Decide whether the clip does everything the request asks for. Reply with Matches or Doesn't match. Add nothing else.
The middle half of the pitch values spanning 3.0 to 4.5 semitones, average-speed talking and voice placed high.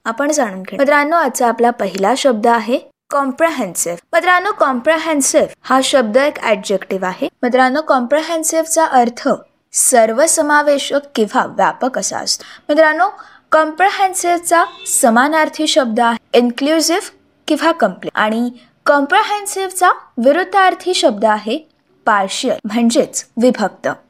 Doesn't match